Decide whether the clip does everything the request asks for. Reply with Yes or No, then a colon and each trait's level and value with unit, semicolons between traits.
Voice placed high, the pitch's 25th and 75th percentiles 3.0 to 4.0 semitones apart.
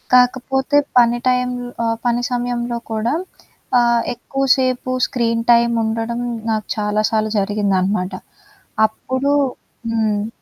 No: high, 235 Hz; narrow, 2.4 semitones